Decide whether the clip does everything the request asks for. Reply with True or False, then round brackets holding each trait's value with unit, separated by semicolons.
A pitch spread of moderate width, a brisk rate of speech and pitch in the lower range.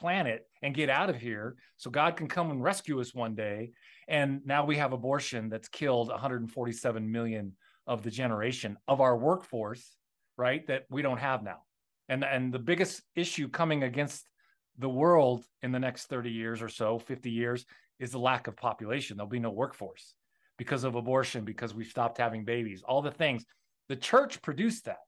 False (3.8 semitones; 185 wpm; 125 Hz)